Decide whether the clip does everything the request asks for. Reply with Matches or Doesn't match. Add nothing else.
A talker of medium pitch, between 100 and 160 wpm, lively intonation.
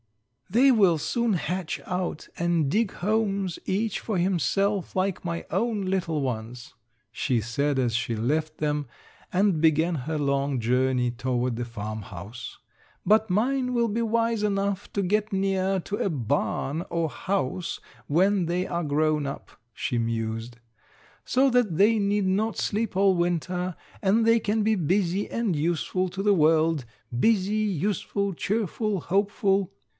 Matches